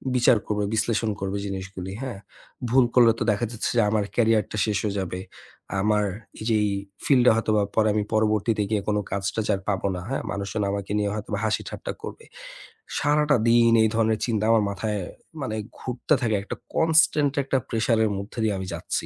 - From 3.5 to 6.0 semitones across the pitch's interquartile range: No, narrow, 2.4 semitones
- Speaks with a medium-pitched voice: No, low, 110 Hz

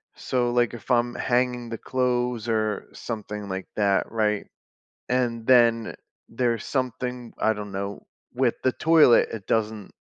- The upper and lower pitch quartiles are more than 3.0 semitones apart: No, narrow, 2.5 semitones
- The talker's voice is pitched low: Yes, low, 115 Hz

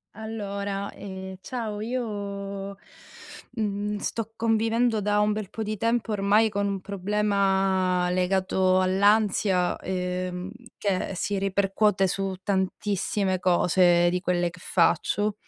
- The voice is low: No, high, 200 Hz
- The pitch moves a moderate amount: No, narrow, 2.0 semitones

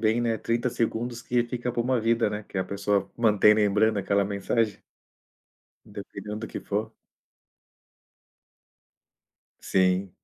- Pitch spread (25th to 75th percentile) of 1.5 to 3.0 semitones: Yes, narrow, 2.6 semitones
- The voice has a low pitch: Yes, low, 110 Hz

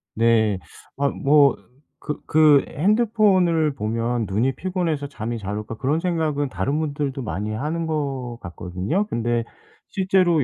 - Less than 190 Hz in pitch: Yes, medium, 140 Hz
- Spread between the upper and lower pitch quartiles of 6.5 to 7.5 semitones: No, wide, 6.0 semitones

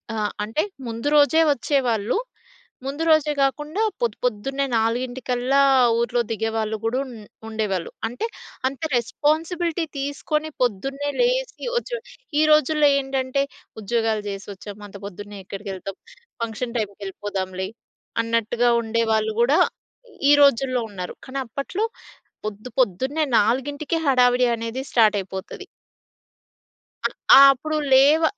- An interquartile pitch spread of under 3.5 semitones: No, average, 4.6 semitones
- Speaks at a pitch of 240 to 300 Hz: Yes, high, 245 Hz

